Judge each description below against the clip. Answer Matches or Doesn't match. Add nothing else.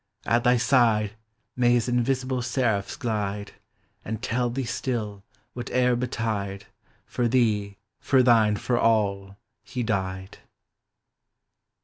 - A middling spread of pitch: Matches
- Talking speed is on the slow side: Matches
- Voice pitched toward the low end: Matches